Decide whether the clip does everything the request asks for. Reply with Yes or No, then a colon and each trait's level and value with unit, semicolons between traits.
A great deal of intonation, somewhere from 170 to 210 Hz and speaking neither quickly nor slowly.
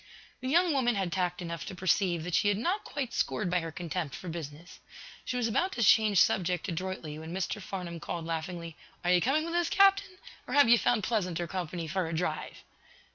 No: wide, 5.9 semitones; medium, 185 Hz; fast, 210 wpm